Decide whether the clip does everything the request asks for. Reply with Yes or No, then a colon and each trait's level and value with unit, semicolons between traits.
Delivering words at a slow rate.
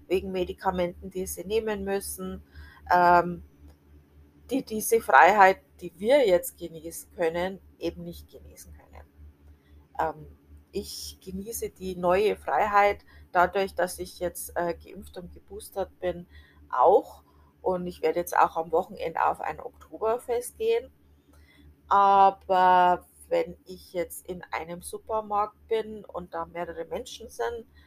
Yes: slow, 120 wpm